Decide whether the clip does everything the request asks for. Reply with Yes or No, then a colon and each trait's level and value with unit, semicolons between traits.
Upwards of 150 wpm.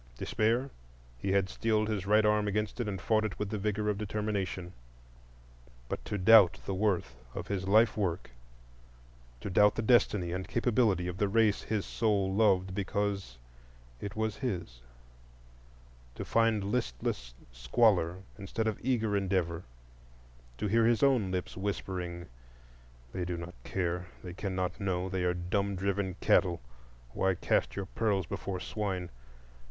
No: average, 145 wpm